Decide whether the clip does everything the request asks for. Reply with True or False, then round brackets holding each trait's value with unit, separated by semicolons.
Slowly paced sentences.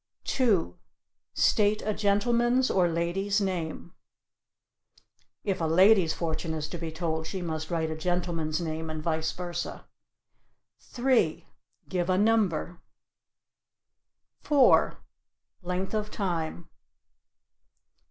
True (110 wpm)